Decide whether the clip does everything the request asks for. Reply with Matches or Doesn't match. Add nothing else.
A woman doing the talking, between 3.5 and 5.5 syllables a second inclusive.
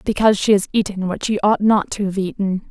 Doesn't match